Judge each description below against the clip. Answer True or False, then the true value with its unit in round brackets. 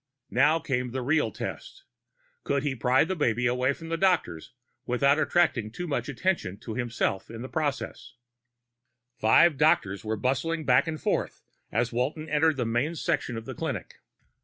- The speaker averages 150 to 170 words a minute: True (165 wpm)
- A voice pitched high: False (130 Hz)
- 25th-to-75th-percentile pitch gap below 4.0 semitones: False (4.7 semitones)